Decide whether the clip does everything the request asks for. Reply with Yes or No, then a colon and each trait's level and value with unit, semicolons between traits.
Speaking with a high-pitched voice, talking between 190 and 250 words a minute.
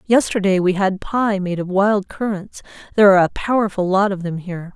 Yes: high, 195 Hz; average, 200 wpm